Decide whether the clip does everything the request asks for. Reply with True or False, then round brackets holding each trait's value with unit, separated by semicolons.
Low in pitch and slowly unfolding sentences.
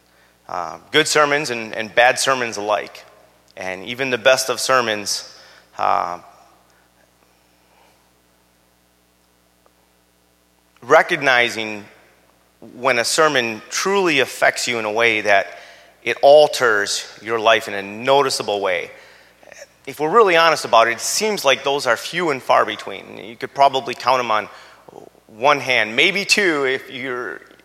True (110 Hz; 130 wpm)